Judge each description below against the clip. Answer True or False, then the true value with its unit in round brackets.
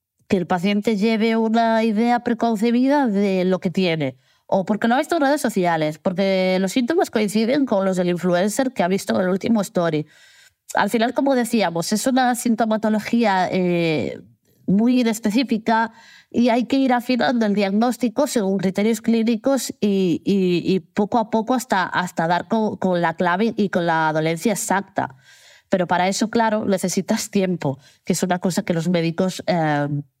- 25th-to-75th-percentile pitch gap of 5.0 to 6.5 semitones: False (4.2 semitones)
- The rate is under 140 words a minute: False (170 wpm)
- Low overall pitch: False (210 Hz)